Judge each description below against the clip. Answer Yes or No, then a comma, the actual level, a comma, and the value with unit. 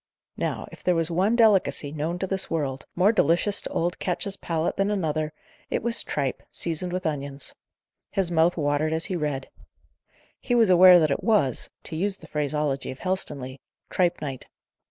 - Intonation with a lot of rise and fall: No, average, 4.2 semitones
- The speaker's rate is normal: Yes, average, 175 wpm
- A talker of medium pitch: Yes, medium, 170 Hz